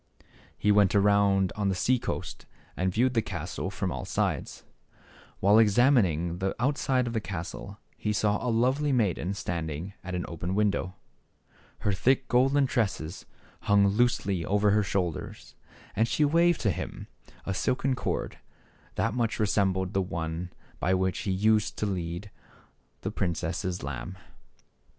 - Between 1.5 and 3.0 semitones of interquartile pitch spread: No, average, 3.8 semitones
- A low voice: Yes, low, 100 Hz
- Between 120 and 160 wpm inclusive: Yes, average, 150 wpm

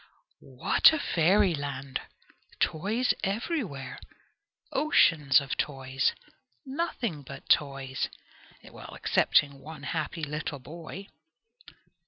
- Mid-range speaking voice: Yes, medium, 155 Hz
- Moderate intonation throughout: No, wide, 6.5 semitones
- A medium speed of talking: No, slow, 80 wpm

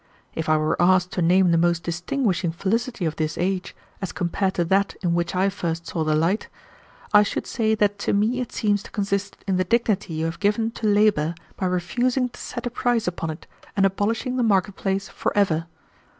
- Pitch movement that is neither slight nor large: Yes, average, 3.6 semitones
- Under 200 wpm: No, fast, 205 wpm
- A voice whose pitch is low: No, high, 195 Hz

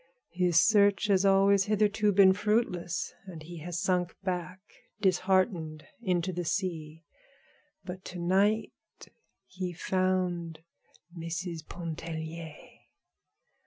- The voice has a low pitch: No, medium, 180 Hz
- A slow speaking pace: Yes, slow, 100 wpm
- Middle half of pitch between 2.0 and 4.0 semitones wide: Yes, narrow, 2.4 semitones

